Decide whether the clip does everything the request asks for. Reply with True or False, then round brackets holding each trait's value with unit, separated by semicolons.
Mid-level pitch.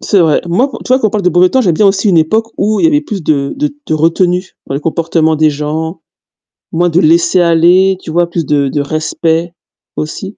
True (170 Hz)